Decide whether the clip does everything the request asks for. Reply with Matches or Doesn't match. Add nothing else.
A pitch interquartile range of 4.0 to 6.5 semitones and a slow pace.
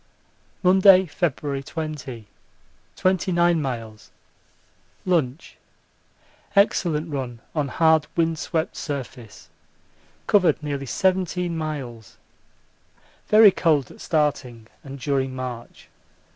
Matches